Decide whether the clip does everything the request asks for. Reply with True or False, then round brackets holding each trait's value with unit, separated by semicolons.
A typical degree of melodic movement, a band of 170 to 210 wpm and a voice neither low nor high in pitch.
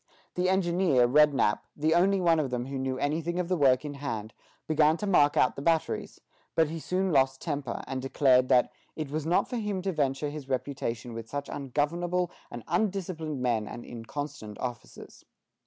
True (4.7 semitones; 185 wpm; 145 Hz)